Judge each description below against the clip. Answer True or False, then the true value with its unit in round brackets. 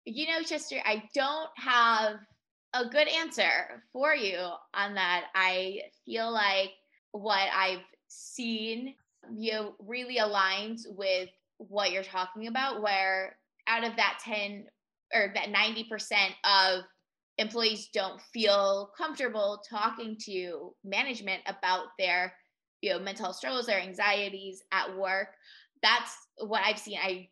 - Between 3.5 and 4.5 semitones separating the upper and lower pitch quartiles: False (3.0 semitones)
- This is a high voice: True (205 Hz)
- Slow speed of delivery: True (130 wpm)